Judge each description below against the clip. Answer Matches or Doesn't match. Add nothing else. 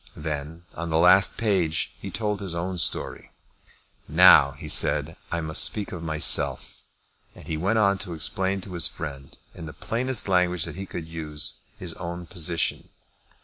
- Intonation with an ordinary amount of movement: Matches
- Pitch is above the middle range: Doesn't match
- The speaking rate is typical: Matches